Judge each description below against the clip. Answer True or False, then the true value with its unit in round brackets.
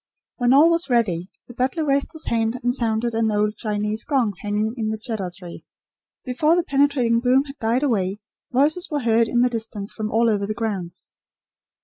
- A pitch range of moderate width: True (3.8 semitones)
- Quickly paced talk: False (195 wpm)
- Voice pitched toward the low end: False (230 Hz)